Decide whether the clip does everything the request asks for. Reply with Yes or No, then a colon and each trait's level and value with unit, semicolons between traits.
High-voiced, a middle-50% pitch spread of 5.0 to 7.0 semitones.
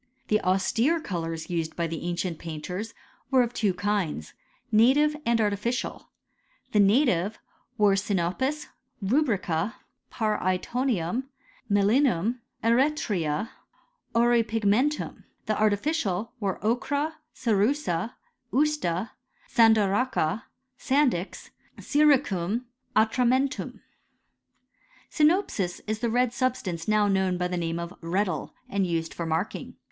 Yes: high, 215 Hz; wide, 5.6 semitones